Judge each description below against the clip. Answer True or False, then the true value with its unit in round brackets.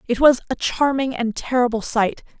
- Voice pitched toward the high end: True (245 Hz)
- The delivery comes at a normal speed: True (175 wpm)